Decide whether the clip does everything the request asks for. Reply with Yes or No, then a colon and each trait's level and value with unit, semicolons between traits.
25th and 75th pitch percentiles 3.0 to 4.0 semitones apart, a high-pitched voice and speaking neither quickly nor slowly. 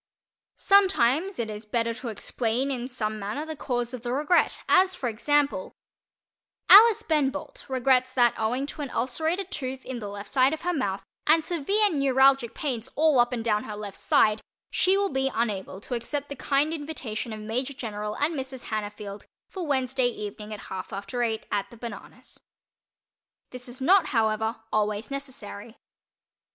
No: average, 4.8 semitones; very high, 255 Hz; average, 170 wpm